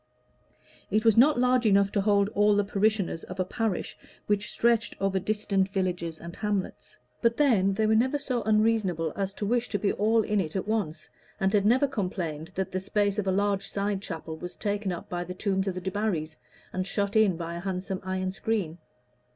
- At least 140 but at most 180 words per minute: No, average, 200 wpm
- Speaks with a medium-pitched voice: No, high, 200 Hz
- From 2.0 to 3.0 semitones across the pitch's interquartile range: Yes, average, 2.7 semitones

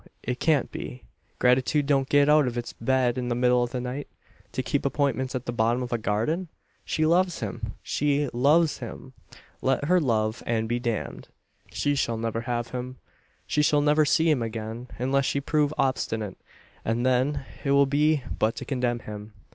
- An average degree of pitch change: Yes, average, 3.5 semitones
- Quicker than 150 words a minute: Yes, average, 185 wpm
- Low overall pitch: Yes, low, 130 Hz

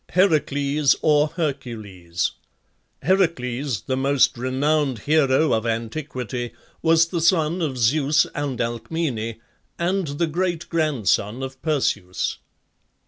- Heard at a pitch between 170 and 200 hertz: No, medium, 140 Hz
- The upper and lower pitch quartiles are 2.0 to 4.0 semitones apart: No, average, 4.6 semitones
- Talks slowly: Yes, slow, 100 wpm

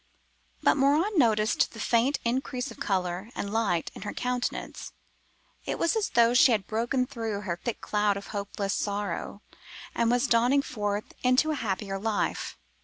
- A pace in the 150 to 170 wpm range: Yes, average, 165 wpm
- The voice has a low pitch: No, high, 225 Hz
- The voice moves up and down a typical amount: Yes, average, 3.7 semitones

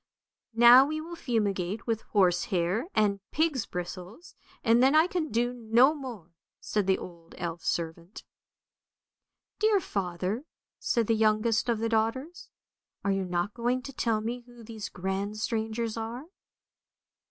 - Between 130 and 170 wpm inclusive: Yes, average, 165 wpm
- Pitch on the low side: No, high, 225 Hz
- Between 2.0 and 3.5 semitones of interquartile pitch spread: No, average, 4.2 semitones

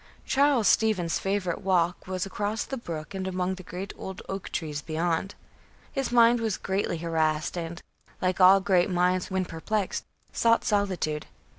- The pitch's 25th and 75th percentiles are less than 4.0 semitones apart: Yes, average, 2.8 semitones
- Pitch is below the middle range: No, medium, 185 Hz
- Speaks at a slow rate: No, average, 155 wpm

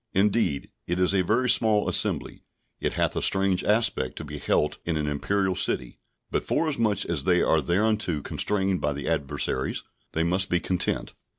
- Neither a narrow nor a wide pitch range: Yes, average, 4.2 semitones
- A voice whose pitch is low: Yes, very low, 95 Hz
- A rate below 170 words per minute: No, average, 175 wpm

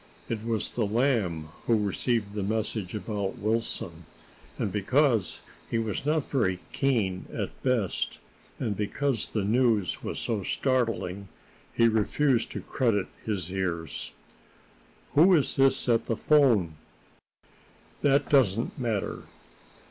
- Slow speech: Yes, slow, 125 wpm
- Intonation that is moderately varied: Yes, average, 4.4 semitones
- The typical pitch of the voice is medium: No, low, 110 Hz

